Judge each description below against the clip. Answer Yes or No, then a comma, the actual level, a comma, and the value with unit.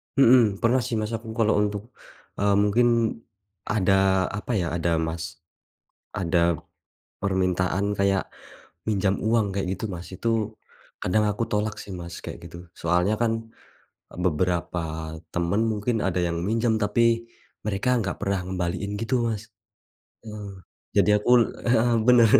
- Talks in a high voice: No, low, 100 Hz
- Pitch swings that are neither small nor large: Yes, average, 3.6 semitones